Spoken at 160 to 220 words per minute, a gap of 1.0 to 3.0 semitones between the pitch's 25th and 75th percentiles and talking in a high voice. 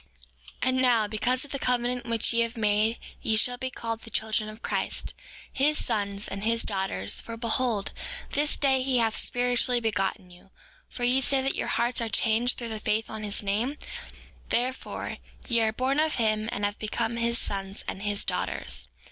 Yes: average, 190 wpm; average, 2.7 semitones; high, 230 Hz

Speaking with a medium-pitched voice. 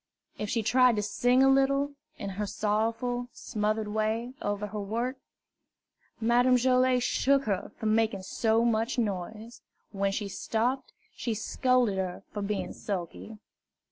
No: high, 225 Hz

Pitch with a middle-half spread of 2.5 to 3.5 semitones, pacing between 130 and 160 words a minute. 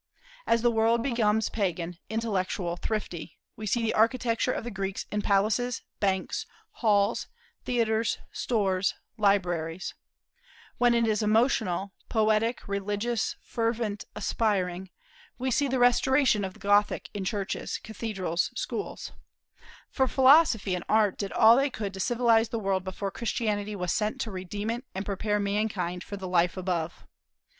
Yes: average, 3.2 semitones; average, 145 wpm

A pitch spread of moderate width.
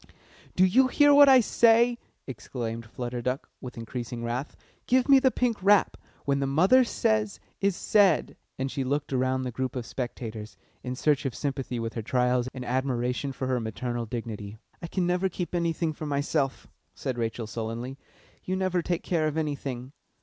No: wide, 6.8 semitones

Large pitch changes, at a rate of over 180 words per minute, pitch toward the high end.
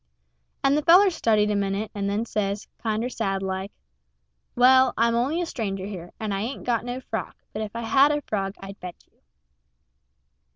No: average, 4.1 semitones; average, 190 wpm; high, 220 Hz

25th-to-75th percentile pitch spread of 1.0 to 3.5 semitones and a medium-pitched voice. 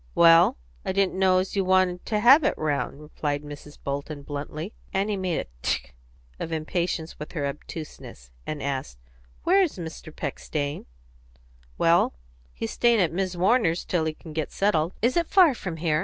No: average, 4.3 semitones; medium, 165 Hz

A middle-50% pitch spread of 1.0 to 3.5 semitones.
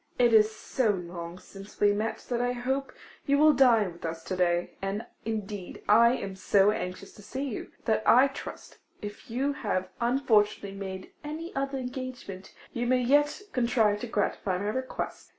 No: average, 4.6 semitones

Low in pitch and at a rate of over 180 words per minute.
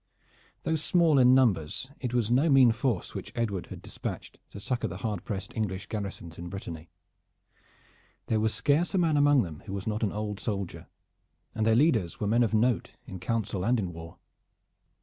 Yes: low, 110 Hz; average, 190 wpm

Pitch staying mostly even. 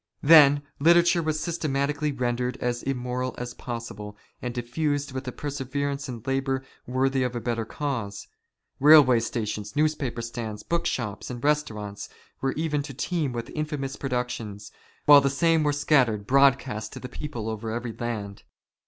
No: average, 3.6 semitones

